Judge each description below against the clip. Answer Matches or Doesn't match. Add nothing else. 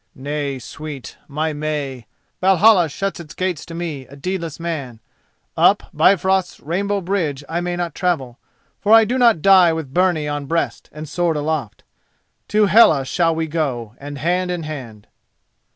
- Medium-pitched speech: Matches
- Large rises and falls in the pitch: Doesn't match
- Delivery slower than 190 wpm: Matches